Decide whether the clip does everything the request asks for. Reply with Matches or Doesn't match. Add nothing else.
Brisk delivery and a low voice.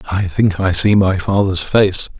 Doesn't match